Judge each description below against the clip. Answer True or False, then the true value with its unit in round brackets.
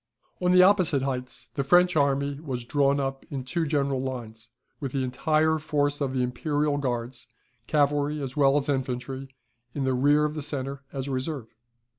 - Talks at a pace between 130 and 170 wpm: False (180 wpm)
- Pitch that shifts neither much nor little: False (2.3 semitones)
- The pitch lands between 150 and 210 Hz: False (140 Hz)